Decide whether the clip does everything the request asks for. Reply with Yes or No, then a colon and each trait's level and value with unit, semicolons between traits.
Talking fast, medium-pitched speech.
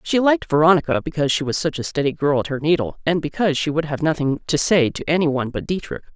Yes: fast, 255 wpm; medium, 155 Hz